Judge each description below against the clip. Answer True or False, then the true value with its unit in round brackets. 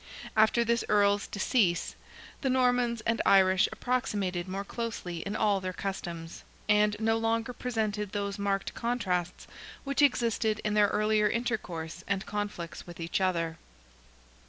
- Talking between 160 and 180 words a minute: False (135 wpm)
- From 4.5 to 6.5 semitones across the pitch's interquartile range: False (3.4 semitones)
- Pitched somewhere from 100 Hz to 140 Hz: False (210 Hz)